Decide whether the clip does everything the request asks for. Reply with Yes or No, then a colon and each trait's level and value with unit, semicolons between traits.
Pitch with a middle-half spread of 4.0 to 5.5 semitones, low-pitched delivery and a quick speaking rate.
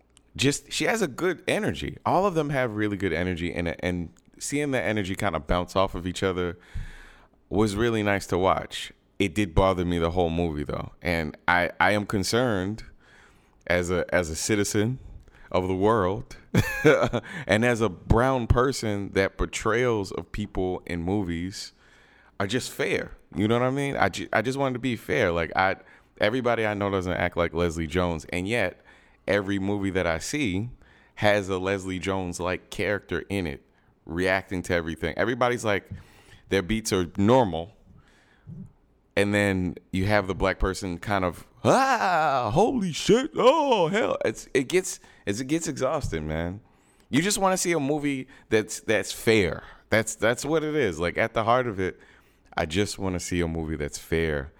No: average, 4.5 semitones; low, 100 Hz; average, 180 wpm